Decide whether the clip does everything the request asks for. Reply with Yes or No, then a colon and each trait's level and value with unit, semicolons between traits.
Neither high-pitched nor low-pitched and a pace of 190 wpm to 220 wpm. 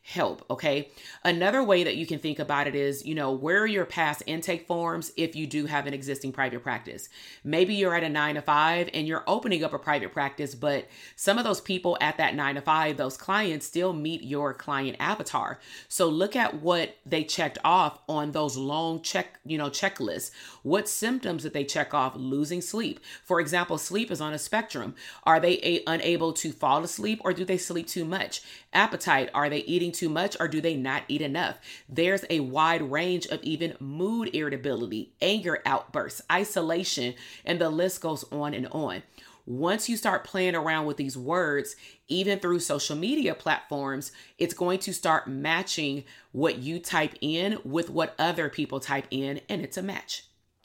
Yes: medium, 160 Hz; average, 195 wpm